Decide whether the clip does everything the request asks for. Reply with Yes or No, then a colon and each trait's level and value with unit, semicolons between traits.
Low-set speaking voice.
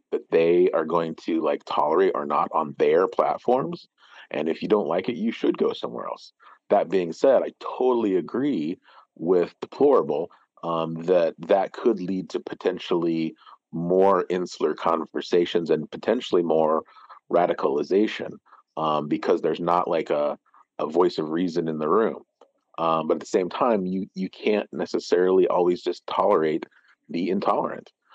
Yes: very low, 95 Hz